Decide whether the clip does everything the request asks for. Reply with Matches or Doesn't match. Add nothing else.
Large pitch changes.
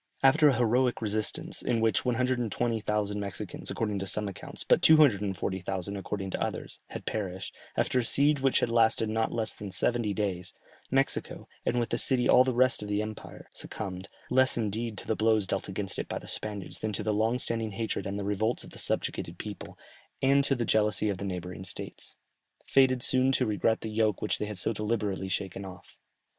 Doesn't match